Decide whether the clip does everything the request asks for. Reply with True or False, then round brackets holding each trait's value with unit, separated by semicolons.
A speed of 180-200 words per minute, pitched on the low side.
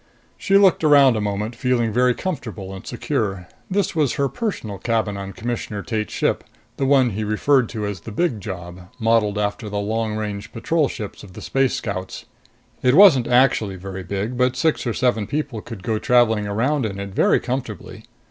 True (185 wpm; 115 Hz)